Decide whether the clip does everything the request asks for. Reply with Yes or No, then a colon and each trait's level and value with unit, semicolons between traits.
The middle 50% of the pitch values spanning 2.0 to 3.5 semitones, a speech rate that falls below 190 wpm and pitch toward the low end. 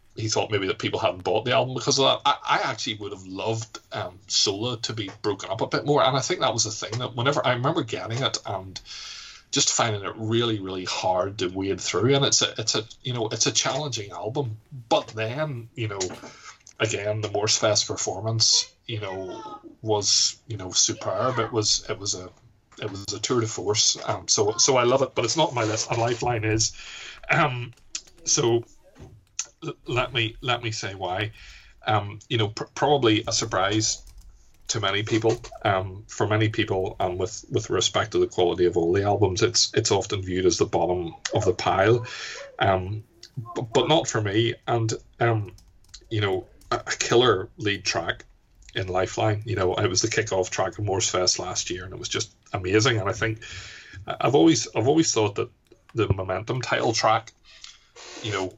No: average, 2.8 semitones; average, 200 wpm; low, 110 Hz